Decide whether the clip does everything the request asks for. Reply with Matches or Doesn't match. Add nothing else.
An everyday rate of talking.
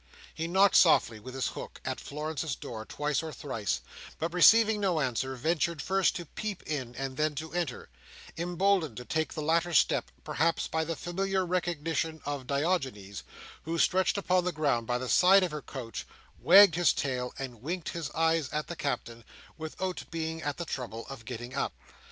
Matches